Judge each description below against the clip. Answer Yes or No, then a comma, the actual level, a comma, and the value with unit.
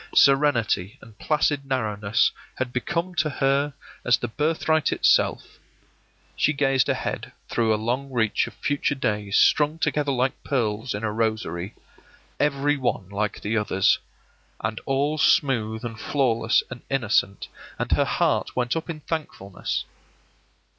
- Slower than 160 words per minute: Yes, average, 140 wpm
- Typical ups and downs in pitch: Yes, average, 4.8 semitones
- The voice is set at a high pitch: No, low, 125 Hz